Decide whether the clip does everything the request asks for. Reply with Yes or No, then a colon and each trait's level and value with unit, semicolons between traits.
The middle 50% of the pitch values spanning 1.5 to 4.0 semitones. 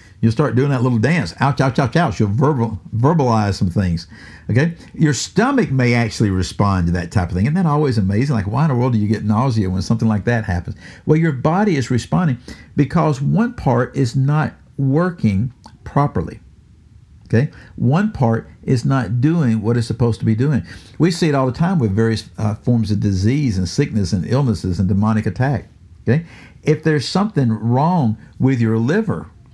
No: average, 5.2 semitones